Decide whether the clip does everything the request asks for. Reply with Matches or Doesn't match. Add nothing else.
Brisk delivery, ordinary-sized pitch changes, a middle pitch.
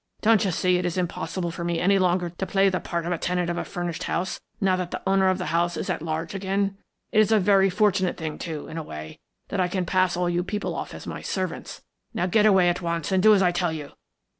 Doesn't match